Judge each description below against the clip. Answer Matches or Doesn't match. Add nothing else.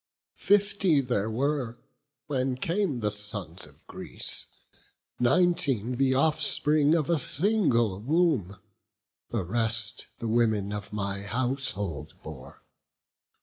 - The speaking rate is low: Matches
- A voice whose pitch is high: Doesn't match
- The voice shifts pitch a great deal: Matches